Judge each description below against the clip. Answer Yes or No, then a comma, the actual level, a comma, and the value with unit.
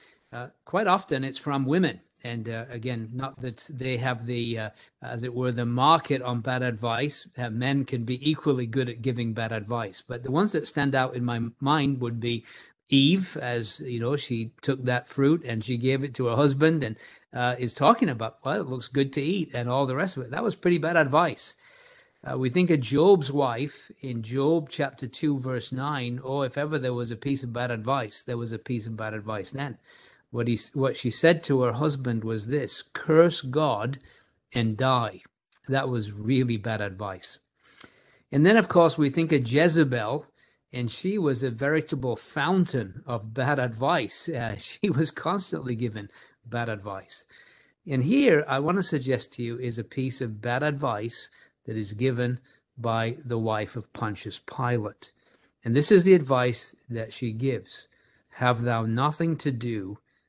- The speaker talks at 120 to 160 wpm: No, average, 190 wpm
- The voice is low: Yes, low, 130 Hz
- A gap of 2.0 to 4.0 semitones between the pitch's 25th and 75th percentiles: Yes, average, 3.7 semitones